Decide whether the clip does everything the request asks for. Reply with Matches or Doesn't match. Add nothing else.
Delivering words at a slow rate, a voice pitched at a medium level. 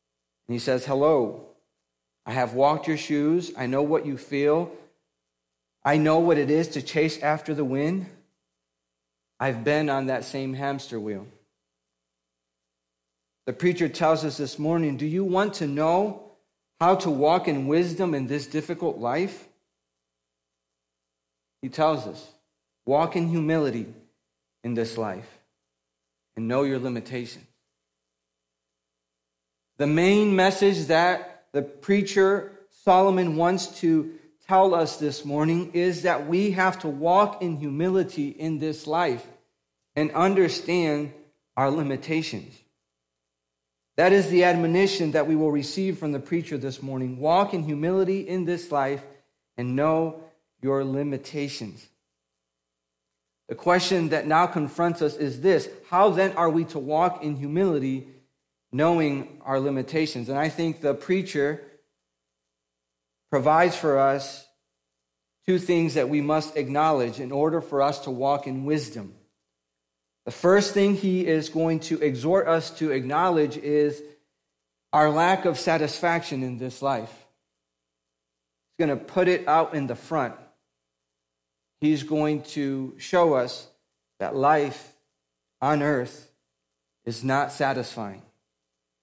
Matches